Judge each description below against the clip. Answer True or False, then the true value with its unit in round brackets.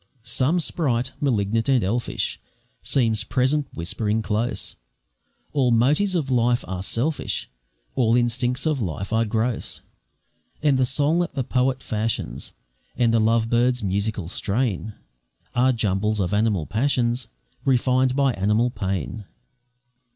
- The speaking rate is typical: False (130 wpm)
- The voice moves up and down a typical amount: True (3.4 semitones)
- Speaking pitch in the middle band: False (120 Hz)